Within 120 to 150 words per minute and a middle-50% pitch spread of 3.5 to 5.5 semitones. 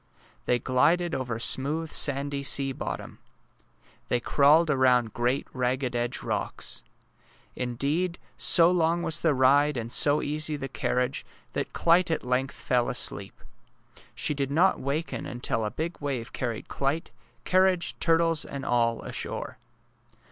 Yes: slow, 135 wpm; average, 4.4 semitones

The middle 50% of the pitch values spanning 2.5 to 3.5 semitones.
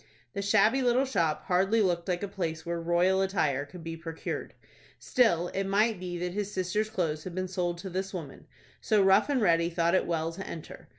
Yes: average, 2.9 semitones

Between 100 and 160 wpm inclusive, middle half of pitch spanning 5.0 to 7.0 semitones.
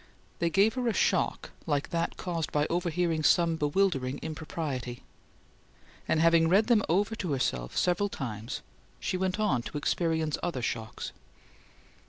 No: average, 145 wpm; average, 4.0 semitones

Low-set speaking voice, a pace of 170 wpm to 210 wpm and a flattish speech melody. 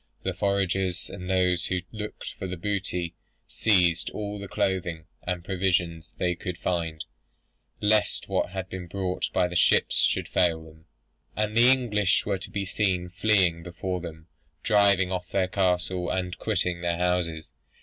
No: very low, 90 Hz; average, 160 wpm; narrow, 2.0 semitones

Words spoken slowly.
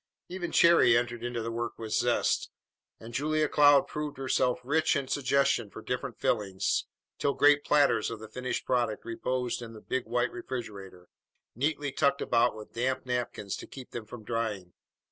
No: average, 170 wpm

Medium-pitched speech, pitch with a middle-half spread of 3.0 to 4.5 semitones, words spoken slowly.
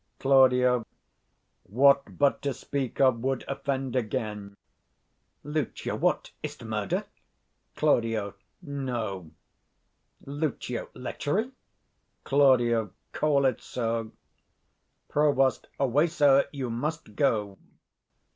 No: low, 130 Hz; average, 3.5 semitones; slow, 90 wpm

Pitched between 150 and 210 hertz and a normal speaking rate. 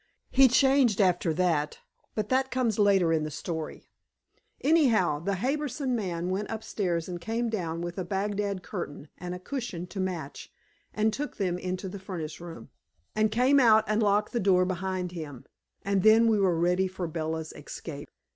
Yes: high, 190 Hz; average, 175 wpm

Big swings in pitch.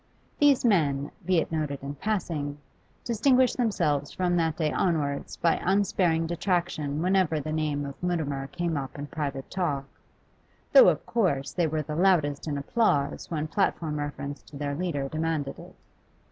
No: average, 3.8 semitones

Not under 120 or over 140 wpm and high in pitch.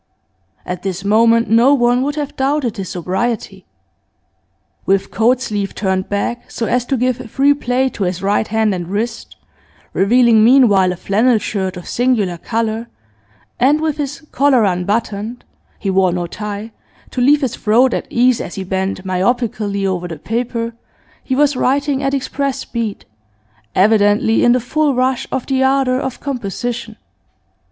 No: average, 160 wpm; high, 230 Hz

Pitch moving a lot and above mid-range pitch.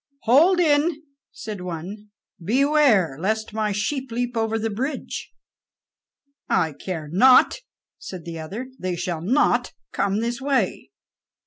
Yes: wide, 6.2 semitones; high, 220 Hz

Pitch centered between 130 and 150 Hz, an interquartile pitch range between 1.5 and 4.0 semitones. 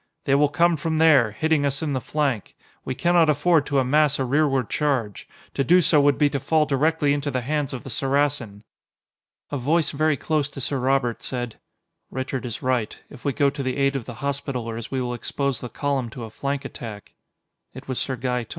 Yes: medium, 140 Hz; average, 2.8 semitones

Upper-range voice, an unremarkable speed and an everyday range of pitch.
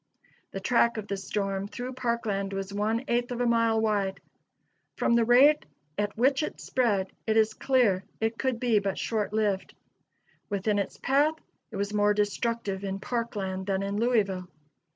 Yes: high, 215 Hz; average, 170 wpm; average, 3.0 semitones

